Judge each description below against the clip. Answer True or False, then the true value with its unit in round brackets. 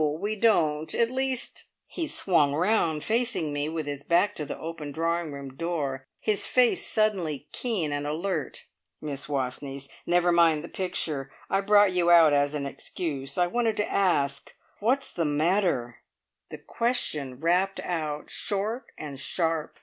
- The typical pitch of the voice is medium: True (165 Hz)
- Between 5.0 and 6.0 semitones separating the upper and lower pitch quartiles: True (5.3 semitones)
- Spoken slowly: False (155 wpm)